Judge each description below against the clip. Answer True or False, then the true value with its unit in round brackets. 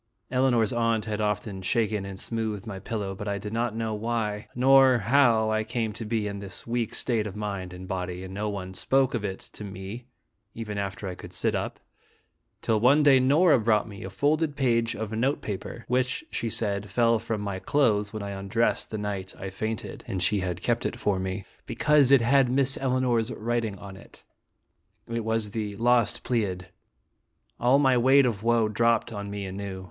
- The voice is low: True (110 Hz)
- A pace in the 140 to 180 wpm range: False (200 wpm)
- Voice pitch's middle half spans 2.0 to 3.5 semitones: True (3.1 semitones)